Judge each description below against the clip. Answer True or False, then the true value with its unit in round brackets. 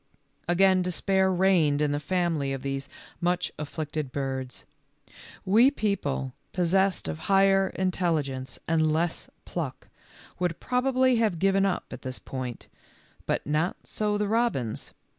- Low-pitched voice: False (175 Hz)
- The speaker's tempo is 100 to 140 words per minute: True (135 wpm)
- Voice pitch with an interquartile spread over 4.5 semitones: True (5.3 semitones)